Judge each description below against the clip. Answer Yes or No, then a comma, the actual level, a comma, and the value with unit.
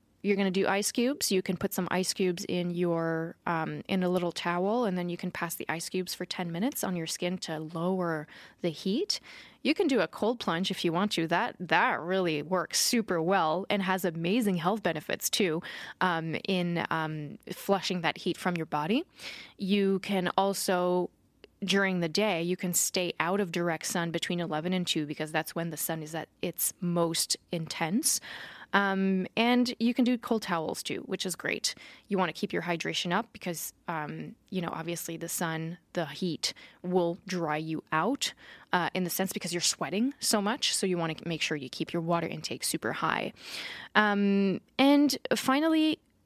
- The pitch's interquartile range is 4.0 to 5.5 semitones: No, average, 2.9 semitones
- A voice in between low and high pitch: Yes, medium, 180 Hz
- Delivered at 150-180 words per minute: No, average, 195 wpm